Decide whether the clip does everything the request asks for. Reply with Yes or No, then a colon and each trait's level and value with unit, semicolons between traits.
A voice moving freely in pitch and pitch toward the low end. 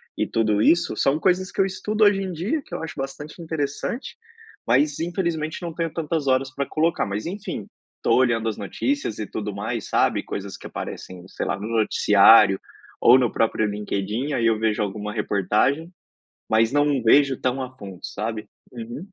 Yes: wide, 7.1 semitones; low, 130 Hz